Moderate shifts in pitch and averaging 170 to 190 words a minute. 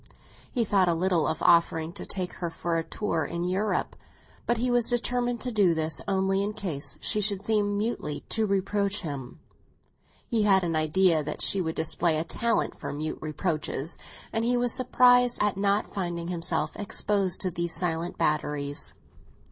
Yes: average, 4.4 semitones; average, 175 wpm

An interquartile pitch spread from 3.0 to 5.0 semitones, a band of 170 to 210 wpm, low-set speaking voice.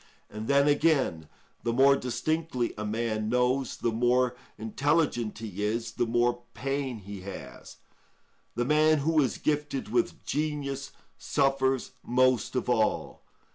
No: average, 3.5 semitones; slow, 135 wpm; low, 125 Hz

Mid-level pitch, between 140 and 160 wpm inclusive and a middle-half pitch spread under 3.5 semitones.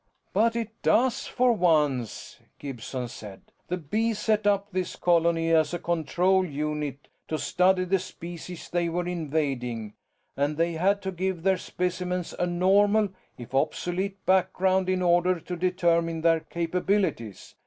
Yes: medium, 175 Hz; average, 145 wpm; average, 3.0 semitones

